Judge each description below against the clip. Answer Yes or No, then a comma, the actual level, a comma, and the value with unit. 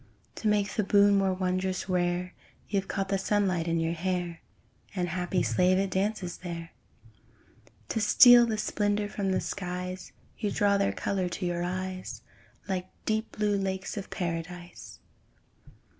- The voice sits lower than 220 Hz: Yes, high, 190 Hz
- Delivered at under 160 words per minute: Yes, average, 150 wpm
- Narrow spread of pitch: Yes, narrow, 2.1 semitones